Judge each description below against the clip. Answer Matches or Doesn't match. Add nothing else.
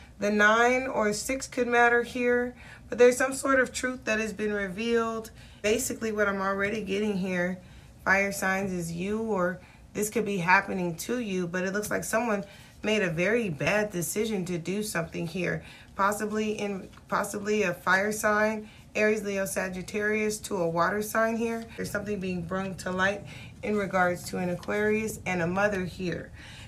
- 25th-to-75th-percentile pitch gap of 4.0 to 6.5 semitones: Doesn't match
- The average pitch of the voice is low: Doesn't match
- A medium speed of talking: Matches